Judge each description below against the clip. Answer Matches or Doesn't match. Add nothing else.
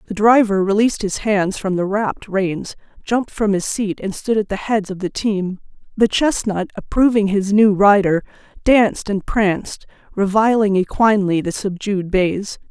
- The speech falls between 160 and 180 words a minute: Matches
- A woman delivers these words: Matches